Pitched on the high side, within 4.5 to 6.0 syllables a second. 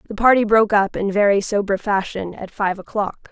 Yes: high, 205 Hz; 5.5 syllables/s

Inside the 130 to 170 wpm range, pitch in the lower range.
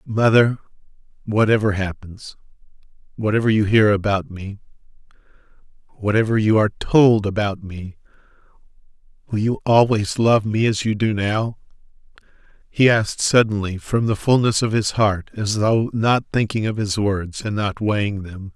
Yes: average, 140 wpm; low, 105 Hz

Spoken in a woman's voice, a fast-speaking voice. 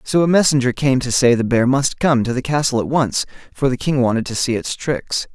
No: male; fast, 260 wpm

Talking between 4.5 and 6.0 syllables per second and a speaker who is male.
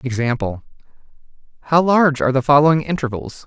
No: 6.5 syllables/s; male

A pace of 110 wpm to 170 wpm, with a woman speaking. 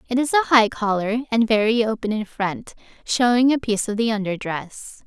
No: average, 200 wpm; female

